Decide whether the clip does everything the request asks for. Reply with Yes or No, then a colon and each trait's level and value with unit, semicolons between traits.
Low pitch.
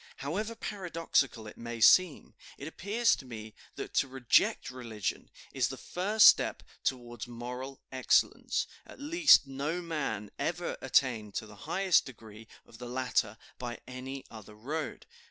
Yes: low, 130 Hz